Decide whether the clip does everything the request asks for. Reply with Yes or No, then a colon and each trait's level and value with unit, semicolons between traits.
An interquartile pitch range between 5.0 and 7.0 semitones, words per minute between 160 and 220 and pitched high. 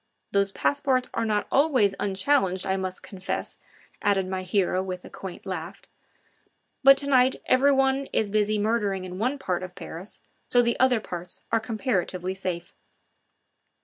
No: average, 5.3 semitones; average, 150 wpm; high, 205 Hz